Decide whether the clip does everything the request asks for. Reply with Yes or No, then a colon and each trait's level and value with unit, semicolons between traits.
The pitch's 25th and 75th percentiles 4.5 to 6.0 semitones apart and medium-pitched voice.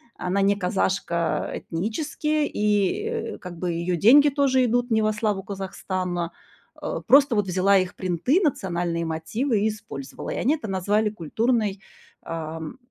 No: average, 5.2 semitones; high, 200 Hz